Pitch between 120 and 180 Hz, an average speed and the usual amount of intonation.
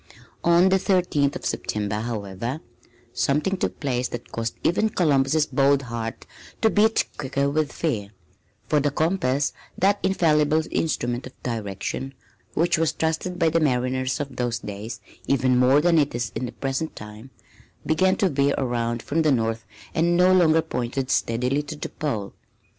Yes: medium, 140 Hz; average, 160 wpm; average, 5.0 semitones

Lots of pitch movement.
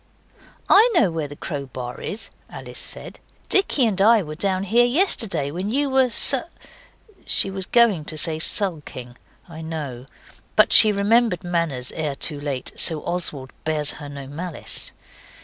Yes: wide, 6.5 semitones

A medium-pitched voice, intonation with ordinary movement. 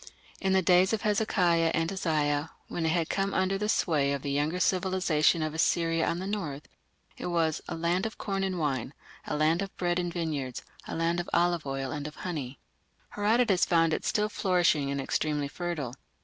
Yes: medium, 170 Hz; average, 3.6 semitones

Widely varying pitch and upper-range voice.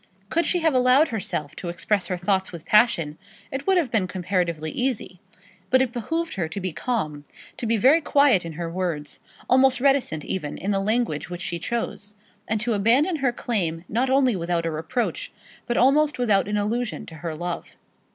Yes: wide, 6.6 semitones; high, 210 Hz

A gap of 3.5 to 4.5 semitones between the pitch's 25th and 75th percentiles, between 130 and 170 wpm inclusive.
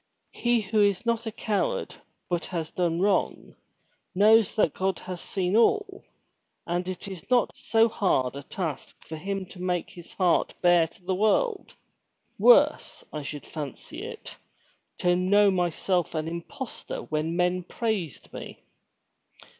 Yes: average, 3.9 semitones; average, 150 wpm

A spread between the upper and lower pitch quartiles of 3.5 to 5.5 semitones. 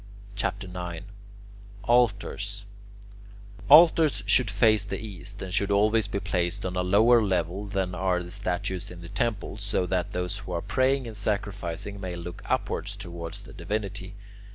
No: narrow, 2.5 semitones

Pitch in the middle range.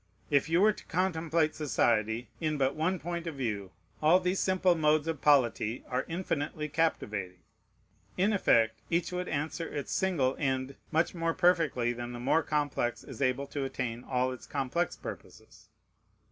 Yes: medium, 150 Hz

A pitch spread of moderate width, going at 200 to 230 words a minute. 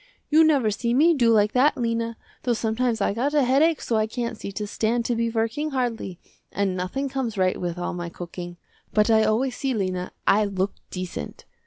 Yes: average, 4.2 semitones; fast, 205 wpm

